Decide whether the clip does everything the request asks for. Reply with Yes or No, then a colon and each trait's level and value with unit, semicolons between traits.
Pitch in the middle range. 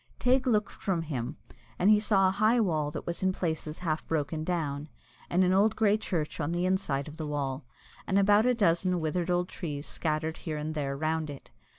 Yes: medium, 165 Hz